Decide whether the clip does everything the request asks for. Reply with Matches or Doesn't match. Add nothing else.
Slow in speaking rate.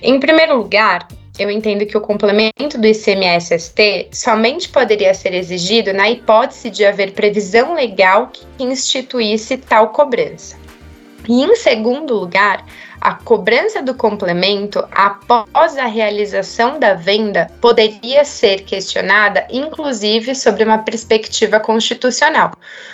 Matches